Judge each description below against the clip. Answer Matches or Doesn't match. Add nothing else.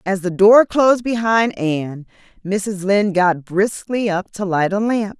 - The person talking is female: Matches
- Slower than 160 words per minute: Doesn't match